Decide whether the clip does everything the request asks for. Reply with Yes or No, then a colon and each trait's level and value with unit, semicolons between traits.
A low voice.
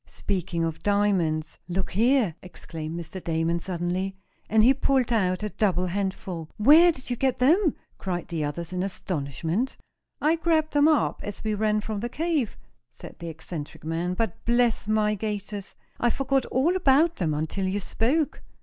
No: high, 205 Hz